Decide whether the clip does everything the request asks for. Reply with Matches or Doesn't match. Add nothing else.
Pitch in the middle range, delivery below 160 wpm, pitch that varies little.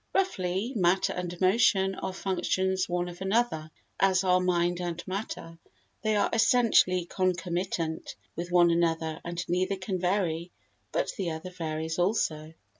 Matches